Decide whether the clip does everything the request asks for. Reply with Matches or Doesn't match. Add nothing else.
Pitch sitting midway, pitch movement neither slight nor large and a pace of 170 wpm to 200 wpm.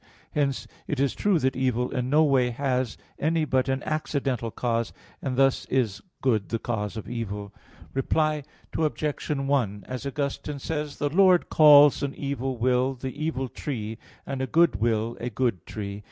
Doesn't match